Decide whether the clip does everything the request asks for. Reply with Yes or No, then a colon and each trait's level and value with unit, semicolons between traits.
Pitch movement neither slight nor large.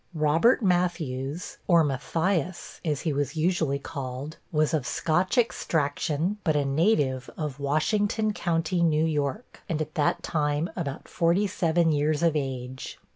Yes: average, 3.3 semitones